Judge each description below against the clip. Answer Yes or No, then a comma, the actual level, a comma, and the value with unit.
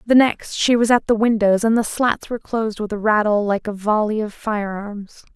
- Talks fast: Yes, fast, 225 wpm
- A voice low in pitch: No, high, 215 Hz